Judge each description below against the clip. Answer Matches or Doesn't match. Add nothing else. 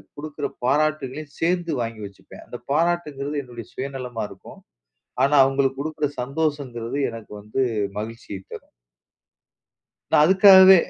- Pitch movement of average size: Matches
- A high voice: Doesn't match